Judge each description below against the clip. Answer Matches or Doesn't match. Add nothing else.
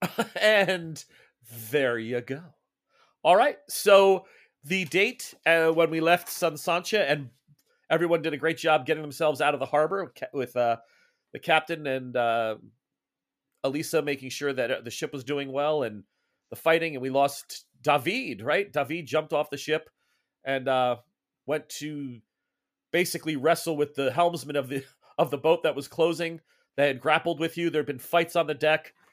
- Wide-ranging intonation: Doesn't match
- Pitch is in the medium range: Matches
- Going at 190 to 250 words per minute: Doesn't match